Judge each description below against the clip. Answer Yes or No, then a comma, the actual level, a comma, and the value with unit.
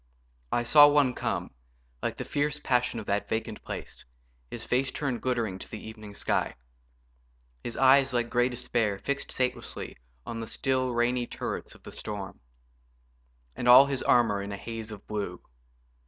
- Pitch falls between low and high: No, low, 120 Hz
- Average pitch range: Yes, average, 3.1 semitones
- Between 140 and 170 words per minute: Yes, average, 165 wpm